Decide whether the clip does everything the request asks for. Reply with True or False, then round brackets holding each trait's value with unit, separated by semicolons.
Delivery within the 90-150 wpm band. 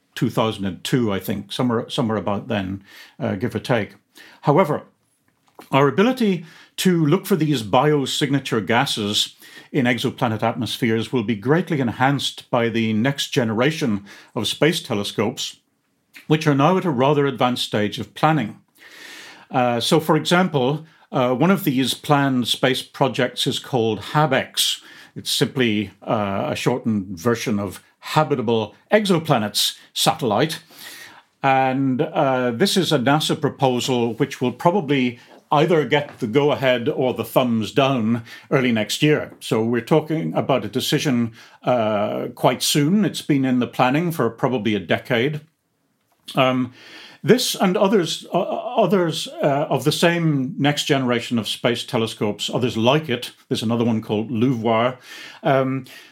True (140 wpm)